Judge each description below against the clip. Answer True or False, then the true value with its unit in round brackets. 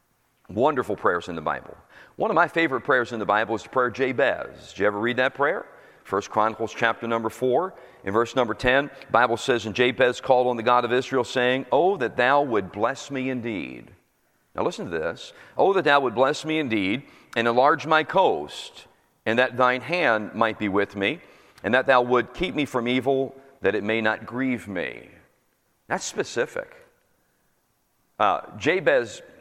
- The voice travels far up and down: False (3.0 semitones)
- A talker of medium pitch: False (125 Hz)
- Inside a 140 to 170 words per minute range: False (190 wpm)